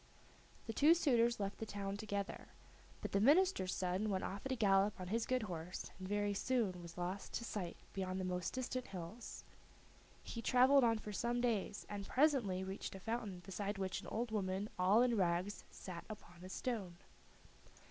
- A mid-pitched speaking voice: No, high, 205 Hz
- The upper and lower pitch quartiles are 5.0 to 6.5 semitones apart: No, average, 3.9 semitones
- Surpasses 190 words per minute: No, average, 185 wpm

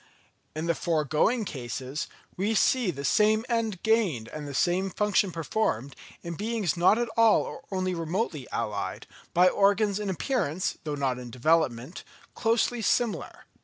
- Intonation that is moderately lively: No, wide, 6.5 semitones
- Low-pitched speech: No, medium, 185 Hz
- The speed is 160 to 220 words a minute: No, average, 150 wpm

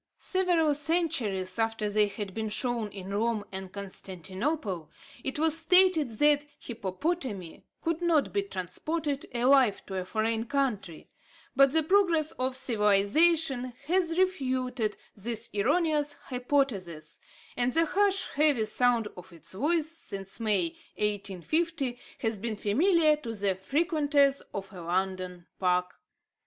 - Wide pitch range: Yes, wide, 7.5 semitones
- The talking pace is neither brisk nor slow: No, slow, 125 wpm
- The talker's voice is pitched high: Yes, high, 245 Hz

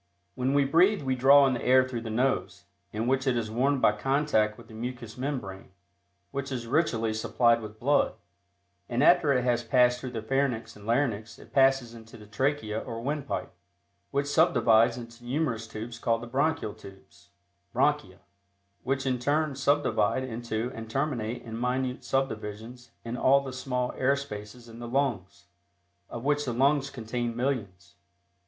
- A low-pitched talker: Yes, low, 125 Hz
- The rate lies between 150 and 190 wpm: Yes, average, 170 wpm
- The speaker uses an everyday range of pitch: Yes, average, 3.2 semitones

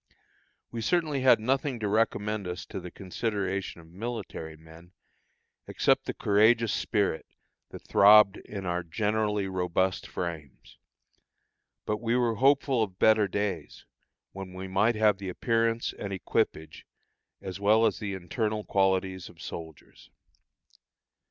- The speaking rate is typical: No, slow, 130 wpm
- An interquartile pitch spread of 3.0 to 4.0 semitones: Yes, average, 3.3 semitones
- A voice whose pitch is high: No, low, 100 Hz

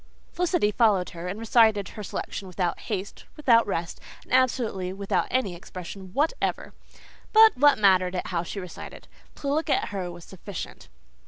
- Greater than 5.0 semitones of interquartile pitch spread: Yes, wide, 5.5 semitones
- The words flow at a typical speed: Yes, average, 160 wpm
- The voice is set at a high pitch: Yes, high, 200 Hz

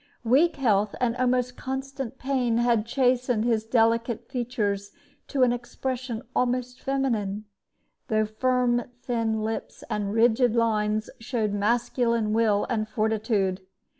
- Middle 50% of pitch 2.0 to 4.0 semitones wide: Yes, narrow, 2.6 semitones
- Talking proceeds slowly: Yes, slow, 120 wpm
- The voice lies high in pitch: Yes, high, 235 Hz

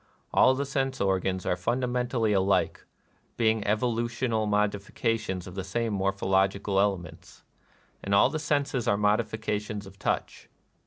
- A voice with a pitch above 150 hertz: No, low, 105 Hz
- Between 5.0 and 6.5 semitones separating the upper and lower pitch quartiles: No, average, 3.4 semitones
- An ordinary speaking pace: Yes, average, 145 wpm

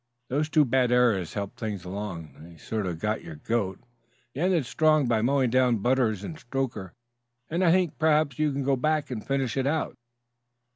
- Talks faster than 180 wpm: Yes, average, 190 wpm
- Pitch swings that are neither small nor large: No, wide, 5.8 semitones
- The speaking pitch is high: No, low, 125 Hz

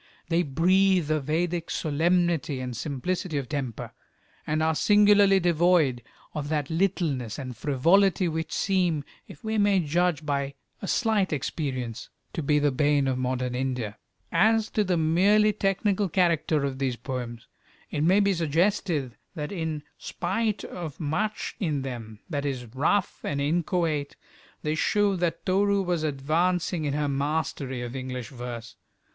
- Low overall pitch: No, medium, 155 Hz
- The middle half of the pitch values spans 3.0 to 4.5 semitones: No, average, 4.9 semitones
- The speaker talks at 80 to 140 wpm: No, average, 150 wpm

